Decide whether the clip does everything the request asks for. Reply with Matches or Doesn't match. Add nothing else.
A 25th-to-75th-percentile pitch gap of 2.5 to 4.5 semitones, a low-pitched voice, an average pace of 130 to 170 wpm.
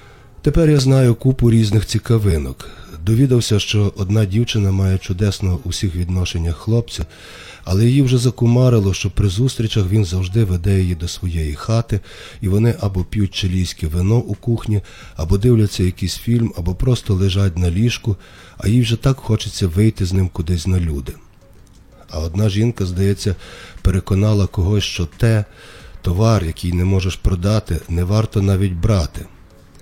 Matches